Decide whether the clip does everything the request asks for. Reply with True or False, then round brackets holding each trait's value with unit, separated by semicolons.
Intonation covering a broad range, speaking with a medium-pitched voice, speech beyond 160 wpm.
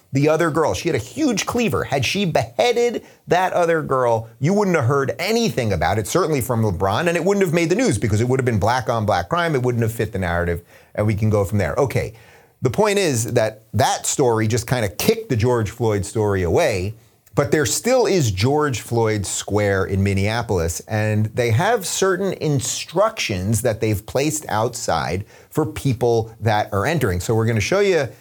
False (6.5 semitones; 120 Hz; 205 wpm)